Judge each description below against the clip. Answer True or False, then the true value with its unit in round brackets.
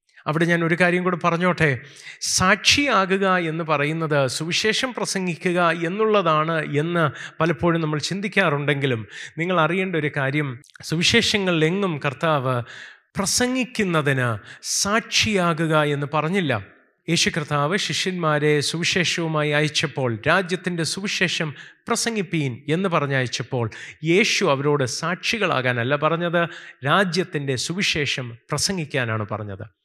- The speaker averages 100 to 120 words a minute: False (90 wpm)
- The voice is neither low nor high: True (160 Hz)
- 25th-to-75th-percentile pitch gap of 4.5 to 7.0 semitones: False (4.0 semitones)